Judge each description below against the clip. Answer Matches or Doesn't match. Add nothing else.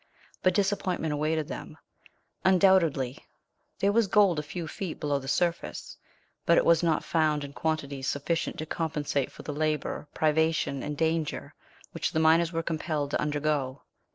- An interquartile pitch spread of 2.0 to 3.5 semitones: Matches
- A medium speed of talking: Matches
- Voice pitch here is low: Doesn't match